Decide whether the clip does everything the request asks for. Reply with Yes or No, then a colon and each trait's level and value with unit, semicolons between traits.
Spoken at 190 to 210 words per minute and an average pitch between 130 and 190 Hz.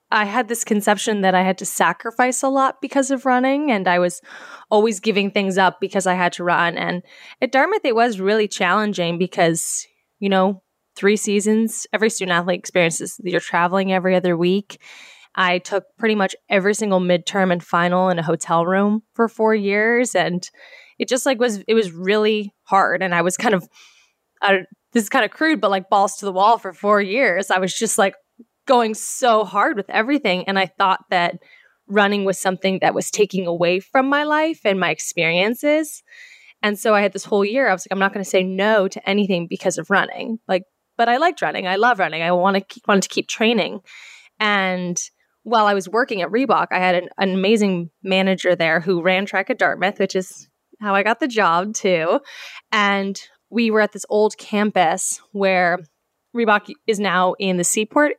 No: average, 200 wpm; high, 200 Hz